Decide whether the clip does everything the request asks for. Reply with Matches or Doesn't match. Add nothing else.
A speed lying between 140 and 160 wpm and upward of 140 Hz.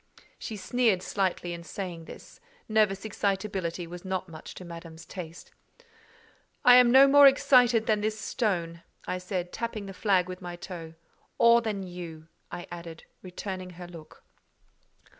Matches